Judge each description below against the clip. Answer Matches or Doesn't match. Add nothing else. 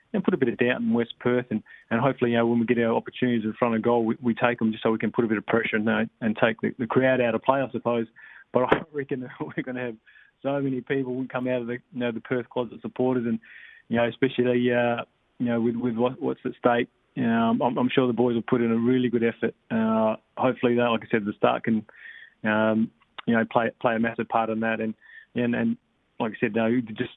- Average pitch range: Doesn't match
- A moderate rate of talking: Doesn't match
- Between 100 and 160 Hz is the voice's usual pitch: Matches